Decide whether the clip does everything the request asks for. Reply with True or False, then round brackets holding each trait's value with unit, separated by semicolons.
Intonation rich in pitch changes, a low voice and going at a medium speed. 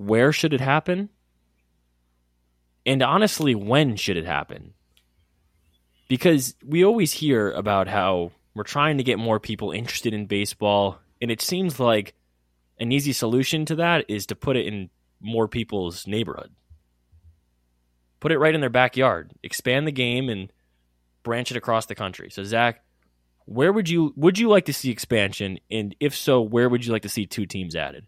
True (7.8 semitones; 110 Hz; 170 wpm)